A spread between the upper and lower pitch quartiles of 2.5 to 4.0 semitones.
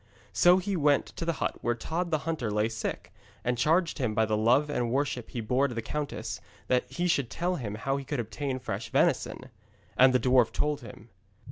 No: average, 4.5 semitones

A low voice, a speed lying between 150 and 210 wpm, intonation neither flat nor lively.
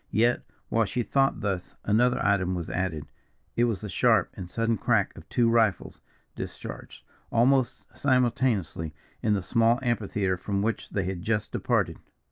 Yes: low, 110 Hz; average, 155 wpm; average, 4.0 semitones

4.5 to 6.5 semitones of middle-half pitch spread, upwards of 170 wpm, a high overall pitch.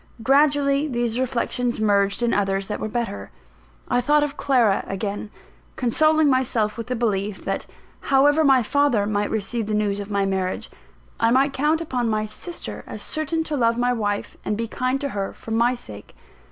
Yes: average, 4.8 semitones; average, 180 wpm; high, 235 Hz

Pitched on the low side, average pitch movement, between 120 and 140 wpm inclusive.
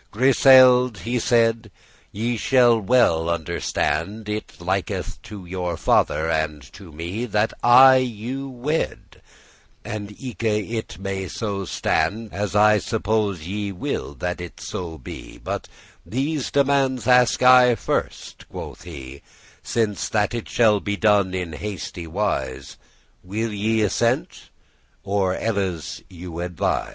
Yes: low, 105 Hz; average, 4.7 semitones; slow, 135 wpm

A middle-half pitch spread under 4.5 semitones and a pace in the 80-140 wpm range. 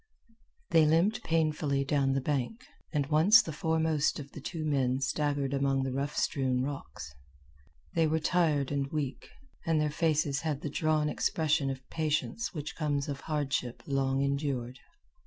No: narrow, 2.4 semitones; average, 155 wpm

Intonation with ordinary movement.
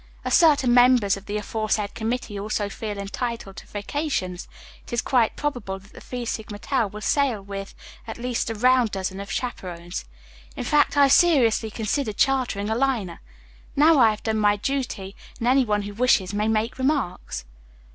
Yes: average, 4.0 semitones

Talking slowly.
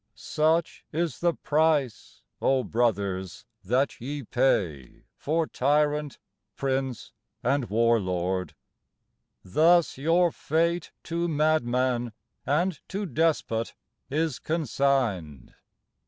Yes: slow, 95 wpm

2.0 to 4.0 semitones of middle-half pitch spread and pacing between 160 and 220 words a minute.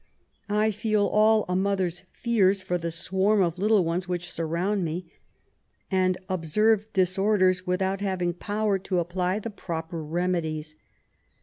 No: average, 2.7 semitones; slow, 135 wpm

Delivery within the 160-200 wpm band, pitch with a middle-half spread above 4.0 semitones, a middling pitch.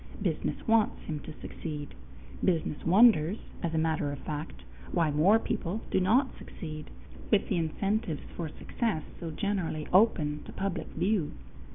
No: average, 150 wpm; average, 4.7 semitones; medium, 170 Hz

